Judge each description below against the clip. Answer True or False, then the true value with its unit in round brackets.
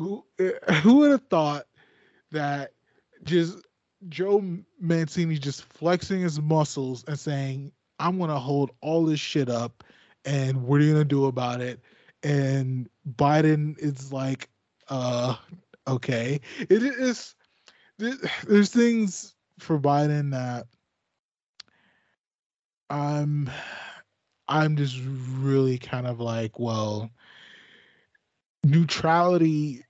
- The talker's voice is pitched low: False (145 Hz)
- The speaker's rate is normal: False (105 wpm)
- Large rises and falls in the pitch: False (4.3 semitones)